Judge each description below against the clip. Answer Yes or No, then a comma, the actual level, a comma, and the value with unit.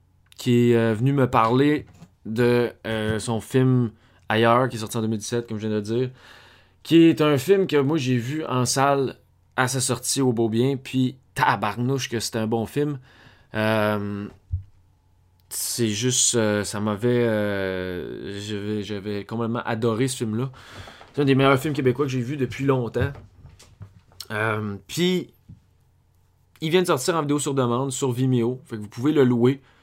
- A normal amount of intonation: Yes, average, 4.0 semitones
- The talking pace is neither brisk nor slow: Yes, average, 175 wpm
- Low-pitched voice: Yes, low, 115 Hz